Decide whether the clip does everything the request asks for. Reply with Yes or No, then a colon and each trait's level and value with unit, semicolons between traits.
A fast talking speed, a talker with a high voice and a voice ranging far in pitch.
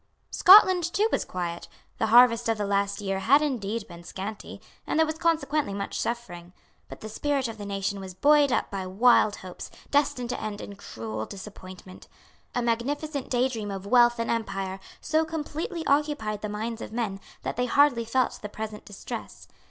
No: average, 180 wpm; high, 225 Hz; wide, 5.9 semitones